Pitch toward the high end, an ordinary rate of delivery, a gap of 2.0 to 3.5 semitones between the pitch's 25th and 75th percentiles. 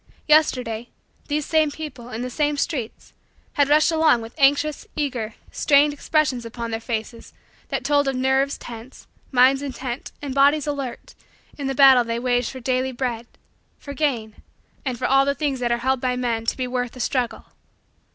Yes: very high, 260 Hz; average, 180 wpm; average, 3.0 semitones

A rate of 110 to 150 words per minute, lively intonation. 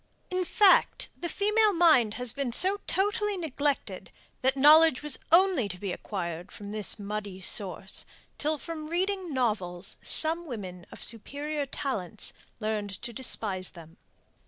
Yes: average, 140 wpm; wide, 8.5 semitones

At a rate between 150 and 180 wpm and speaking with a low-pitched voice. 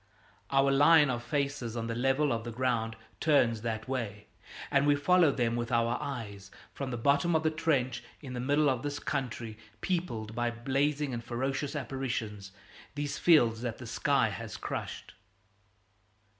Yes: average, 165 wpm; low, 130 Hz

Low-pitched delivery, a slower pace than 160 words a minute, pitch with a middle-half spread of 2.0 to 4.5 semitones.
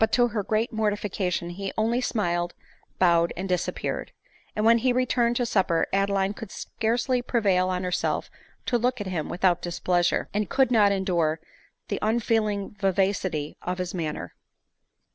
No: high, 200 Hz; average, 150 wpm; average, 3.8 semitones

